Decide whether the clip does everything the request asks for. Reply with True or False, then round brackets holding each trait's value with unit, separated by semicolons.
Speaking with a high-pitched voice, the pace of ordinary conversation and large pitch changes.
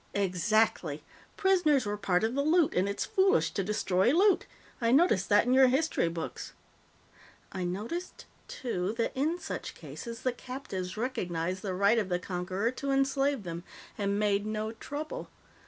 True (220 Hz; 160 wpm; 6.5 semitones)